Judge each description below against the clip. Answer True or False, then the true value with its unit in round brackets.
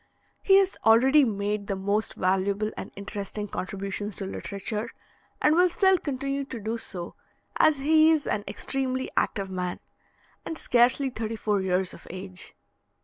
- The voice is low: False (215 Hz)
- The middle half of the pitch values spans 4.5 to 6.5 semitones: True (5.5 semitones)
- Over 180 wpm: False (150 wpm)